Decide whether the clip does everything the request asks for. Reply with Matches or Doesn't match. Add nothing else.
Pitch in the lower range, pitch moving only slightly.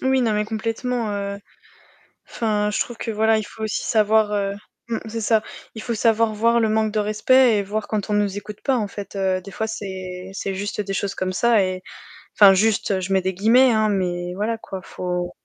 Doesn't match